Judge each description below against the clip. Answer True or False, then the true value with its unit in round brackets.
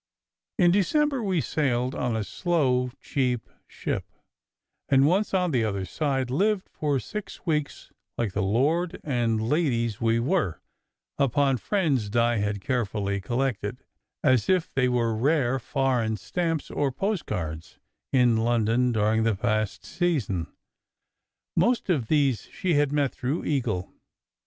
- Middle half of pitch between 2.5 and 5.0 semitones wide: False (5.6 semitones)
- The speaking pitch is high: False (130 Hz)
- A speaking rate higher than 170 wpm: False (135 wpm)